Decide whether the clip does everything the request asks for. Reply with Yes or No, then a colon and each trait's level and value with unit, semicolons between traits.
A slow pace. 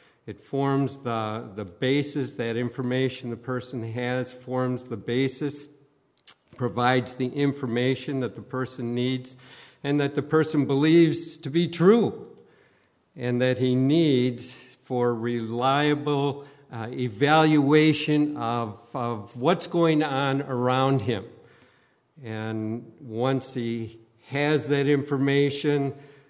Yes: slow, 110 wpm